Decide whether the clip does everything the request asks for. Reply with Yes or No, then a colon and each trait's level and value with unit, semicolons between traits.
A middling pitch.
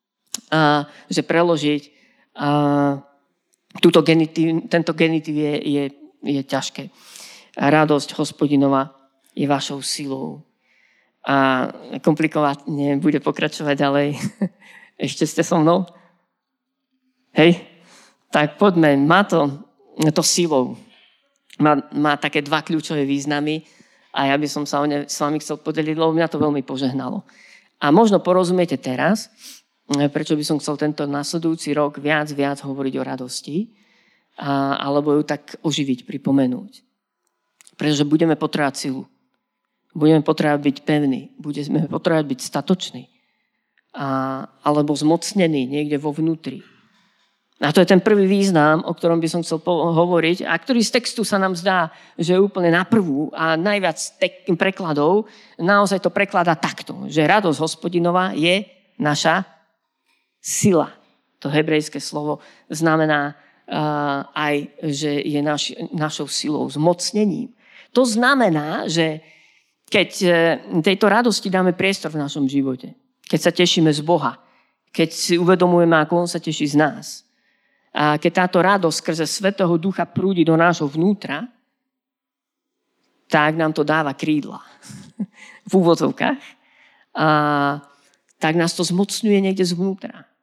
Yes: medium, 160 Hz